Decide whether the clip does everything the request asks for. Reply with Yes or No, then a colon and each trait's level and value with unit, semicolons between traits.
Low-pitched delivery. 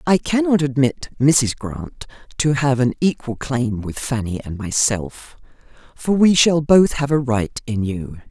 Yes: low, 130 Hz